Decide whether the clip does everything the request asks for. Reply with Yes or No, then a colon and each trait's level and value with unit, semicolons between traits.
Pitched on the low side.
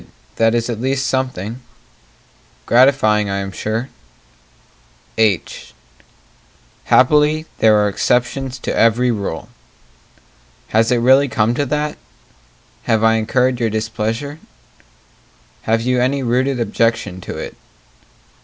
Yes: low, 120 Hz